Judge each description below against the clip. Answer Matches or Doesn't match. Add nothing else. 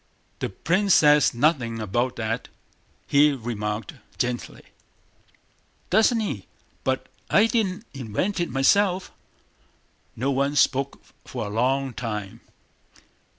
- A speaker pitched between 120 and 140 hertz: Matches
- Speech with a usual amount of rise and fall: Doesn't match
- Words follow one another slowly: Matches